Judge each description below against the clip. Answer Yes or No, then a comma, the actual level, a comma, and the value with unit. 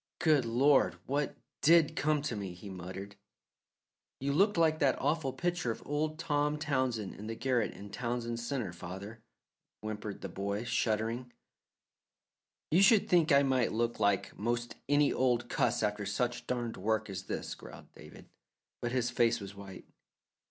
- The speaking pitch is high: No, low, 120 Hz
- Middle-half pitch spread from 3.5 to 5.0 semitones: No, wide, 5.5 semitones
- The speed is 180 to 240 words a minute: No, average, 155 wpm